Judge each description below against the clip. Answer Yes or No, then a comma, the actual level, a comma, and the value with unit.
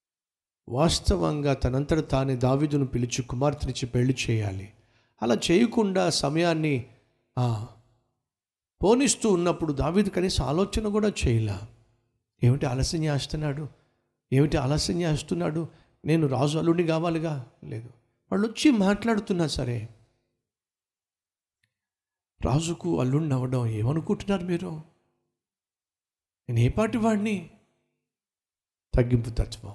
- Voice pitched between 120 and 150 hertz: Yes, low, 135 Hz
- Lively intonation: Yes, wide, 6.2 semitones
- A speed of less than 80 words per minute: No, average, 85 wpm